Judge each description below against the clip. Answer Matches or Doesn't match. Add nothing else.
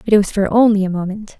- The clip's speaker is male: Doesn't match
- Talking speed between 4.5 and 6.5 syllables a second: Doesn't match